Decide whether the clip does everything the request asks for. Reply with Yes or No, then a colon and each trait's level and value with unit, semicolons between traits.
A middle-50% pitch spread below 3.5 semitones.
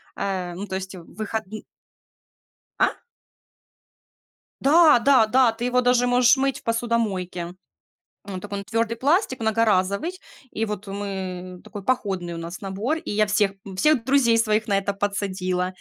No: average, 4.1 semitones